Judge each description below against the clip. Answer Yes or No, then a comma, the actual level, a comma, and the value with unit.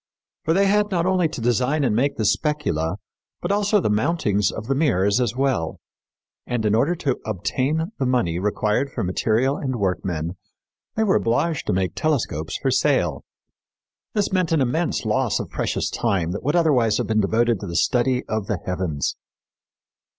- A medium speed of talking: Yes, average, 180 wpm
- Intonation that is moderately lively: No, wide, 7.2 semitones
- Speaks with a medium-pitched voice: No, low, 120 Hz